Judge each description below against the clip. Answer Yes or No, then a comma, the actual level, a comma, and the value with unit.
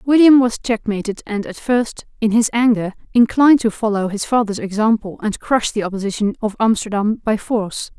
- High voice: Yes, high, 220 Hz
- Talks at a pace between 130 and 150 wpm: No, average, 175 wpm